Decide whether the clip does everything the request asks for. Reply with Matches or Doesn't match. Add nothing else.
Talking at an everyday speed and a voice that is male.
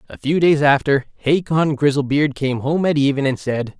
Matches